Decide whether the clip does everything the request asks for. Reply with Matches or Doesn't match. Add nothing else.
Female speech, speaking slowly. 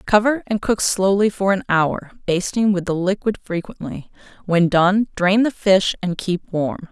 Doesn't match